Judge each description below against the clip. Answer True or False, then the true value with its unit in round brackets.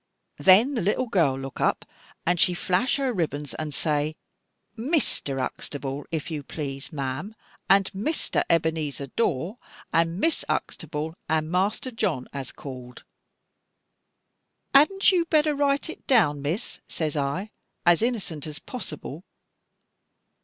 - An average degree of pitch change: False (7.6 semitones)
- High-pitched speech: False (165 Hz)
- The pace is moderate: False (130 wpm)